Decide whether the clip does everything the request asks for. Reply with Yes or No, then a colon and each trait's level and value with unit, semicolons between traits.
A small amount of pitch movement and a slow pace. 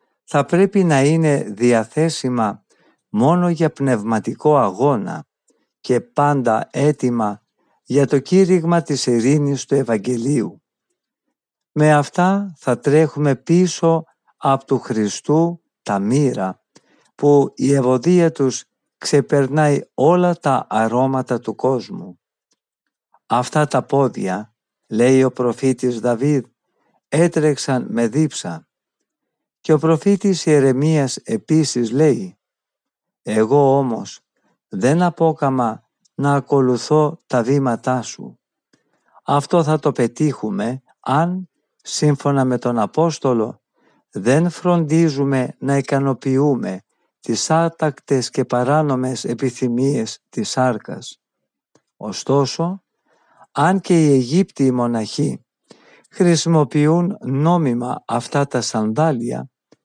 No: average, 4.1 semitones; slow, 95 wpm